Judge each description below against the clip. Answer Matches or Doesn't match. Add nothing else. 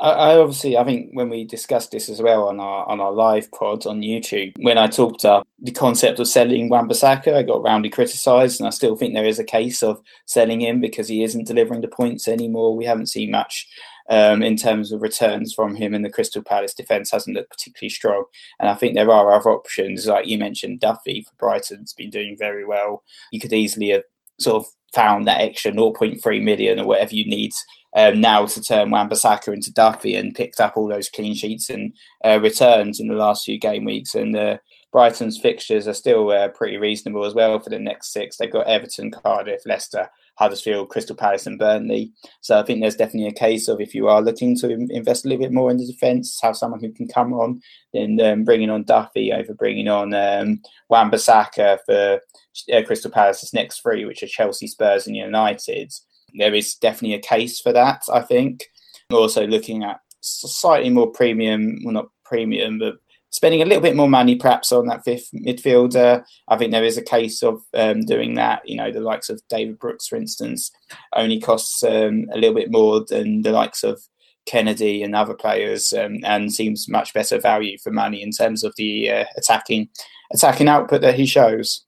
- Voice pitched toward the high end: Doesn't match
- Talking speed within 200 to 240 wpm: Matches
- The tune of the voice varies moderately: Doesn't match